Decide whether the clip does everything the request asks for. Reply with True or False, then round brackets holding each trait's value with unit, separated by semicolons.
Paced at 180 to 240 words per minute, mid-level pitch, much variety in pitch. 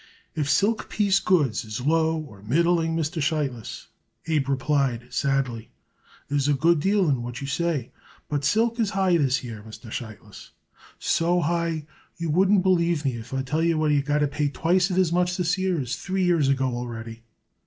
False (185 wpm; 150 Hz; 4.7 semitones)